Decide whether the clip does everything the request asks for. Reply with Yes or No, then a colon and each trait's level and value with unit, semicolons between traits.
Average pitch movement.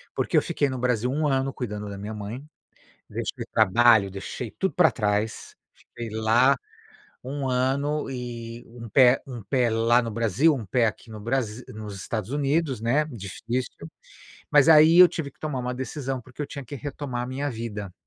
Yes: average, 3.6 semitones